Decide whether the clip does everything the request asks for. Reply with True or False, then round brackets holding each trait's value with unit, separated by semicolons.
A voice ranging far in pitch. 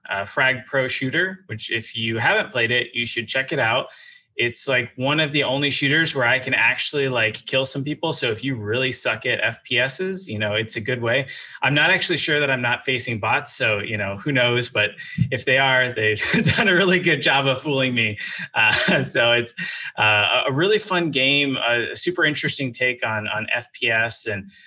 False (3.8 semitones)